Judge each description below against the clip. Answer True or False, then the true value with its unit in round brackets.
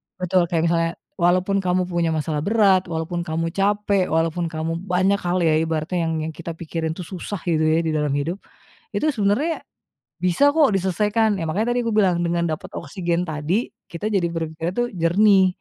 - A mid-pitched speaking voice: True (175 Hz)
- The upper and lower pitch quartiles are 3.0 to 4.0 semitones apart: True (3.3 semitones)